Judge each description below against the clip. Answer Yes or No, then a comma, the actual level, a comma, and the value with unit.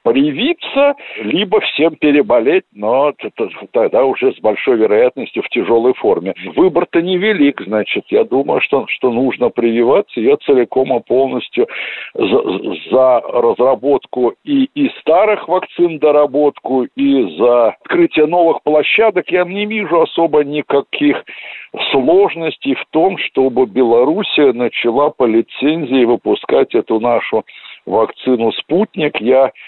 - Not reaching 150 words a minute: Yes, average, 115 wpm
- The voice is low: No, medium, 180 Hz